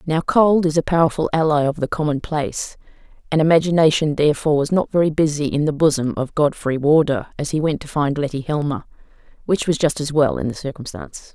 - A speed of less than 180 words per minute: No, average, 195 wpm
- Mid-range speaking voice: Yes, medium, 150 Hz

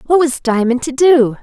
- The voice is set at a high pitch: Yes, very high, 270 Hz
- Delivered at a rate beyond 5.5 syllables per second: No, 4.8 syllables/s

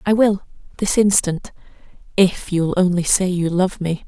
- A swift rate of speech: No, average, 145 wpm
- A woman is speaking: Yes, female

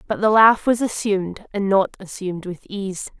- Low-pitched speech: No, high, 200 Hz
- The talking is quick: No, average, 190 wpm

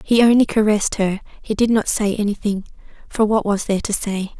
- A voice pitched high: Yes, high, 210 Hz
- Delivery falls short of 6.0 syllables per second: No, 6.1 syllables/s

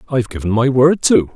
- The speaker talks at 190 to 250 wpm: No, fast, 265 wpm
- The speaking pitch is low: Yes, low, 125 Hz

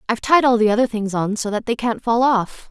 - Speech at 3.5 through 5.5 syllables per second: No, 5.9 syllables/s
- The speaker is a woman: Yes, female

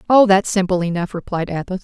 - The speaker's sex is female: Yes, female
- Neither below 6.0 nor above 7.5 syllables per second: Yes, 6.1 syllables/s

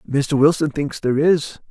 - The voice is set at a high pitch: No, medium, 145 Hz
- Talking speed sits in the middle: Yes, average, 175 wpm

